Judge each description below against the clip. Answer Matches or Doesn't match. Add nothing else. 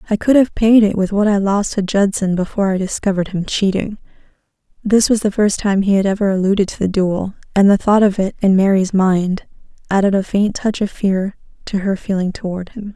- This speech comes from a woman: Matches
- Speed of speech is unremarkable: Doesn't match